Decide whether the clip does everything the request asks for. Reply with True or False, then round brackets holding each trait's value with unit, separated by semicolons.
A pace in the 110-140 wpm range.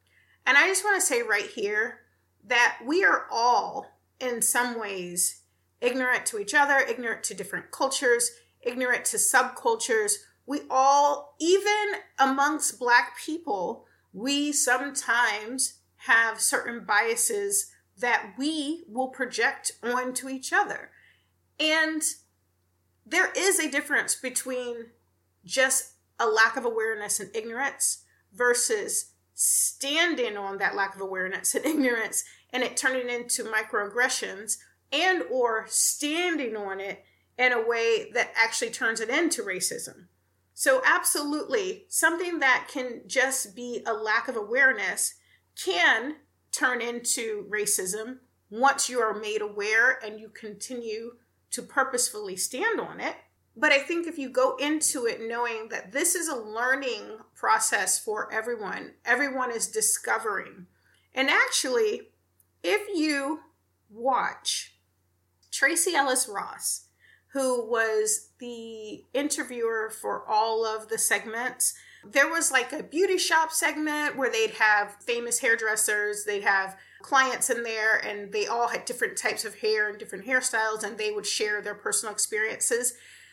True (135 wpm)